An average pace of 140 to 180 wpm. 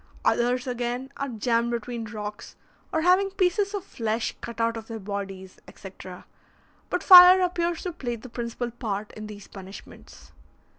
Yes: average, 155 wpm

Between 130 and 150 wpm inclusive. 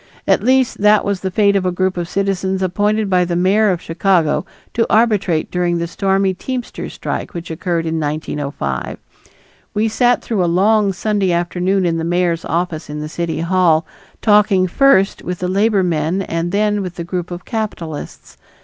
No: average, 180 wpm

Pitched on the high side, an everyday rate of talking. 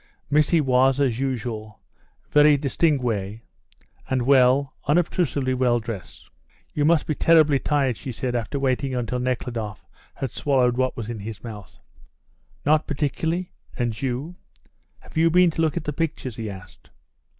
No: low, 130 Hz; average, 150 wpm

